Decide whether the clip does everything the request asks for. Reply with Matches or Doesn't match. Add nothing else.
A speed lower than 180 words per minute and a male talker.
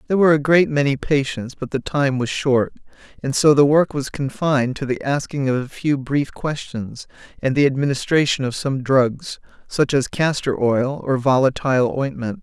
Doesn't match